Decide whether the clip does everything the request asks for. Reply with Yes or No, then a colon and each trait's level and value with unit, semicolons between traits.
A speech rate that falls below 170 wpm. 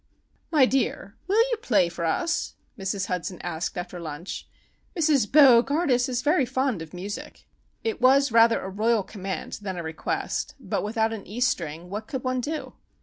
No: average, 175 wpm